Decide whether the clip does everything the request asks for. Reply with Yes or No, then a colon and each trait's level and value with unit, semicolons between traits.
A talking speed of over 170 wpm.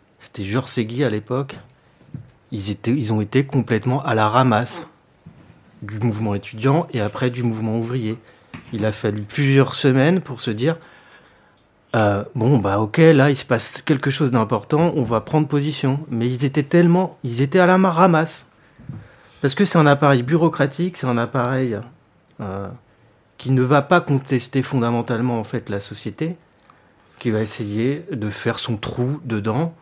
No: average, 165 wpm